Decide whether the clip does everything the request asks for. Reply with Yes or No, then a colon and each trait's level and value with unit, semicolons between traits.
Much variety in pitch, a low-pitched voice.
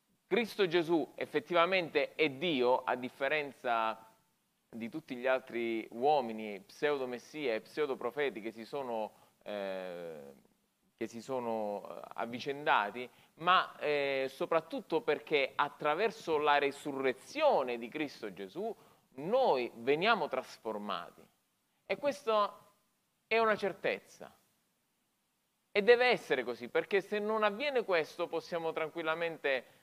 No: wide, 7.8 semitones; medium, 150 Hz